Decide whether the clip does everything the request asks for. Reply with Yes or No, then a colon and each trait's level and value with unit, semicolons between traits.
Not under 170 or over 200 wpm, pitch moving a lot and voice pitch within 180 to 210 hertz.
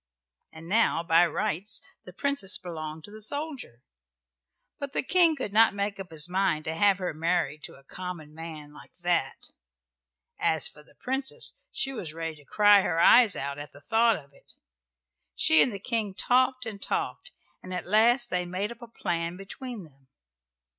Yes: average, 185 wpm; wide, 5.8 semitones; medium, 185 Hz